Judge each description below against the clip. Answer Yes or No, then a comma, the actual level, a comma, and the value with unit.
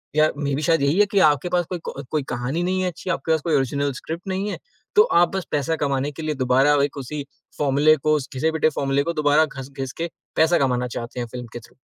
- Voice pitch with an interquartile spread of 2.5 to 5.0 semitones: Yes, average, 3.1 semitones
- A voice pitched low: No, medium, 150 Hz